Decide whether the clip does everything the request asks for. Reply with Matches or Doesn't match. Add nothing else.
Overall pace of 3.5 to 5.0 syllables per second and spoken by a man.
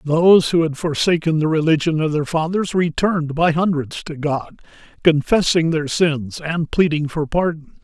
Matches